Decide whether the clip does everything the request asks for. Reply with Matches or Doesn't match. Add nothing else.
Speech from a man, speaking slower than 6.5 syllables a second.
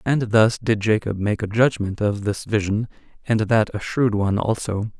Matches